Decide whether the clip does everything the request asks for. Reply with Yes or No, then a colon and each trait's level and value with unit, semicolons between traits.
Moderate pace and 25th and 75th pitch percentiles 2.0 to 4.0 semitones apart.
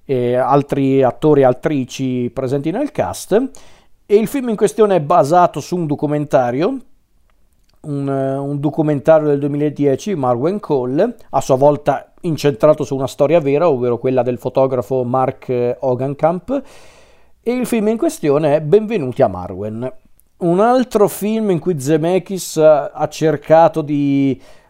No: average, 140 wpm; wide, 5.4 semitones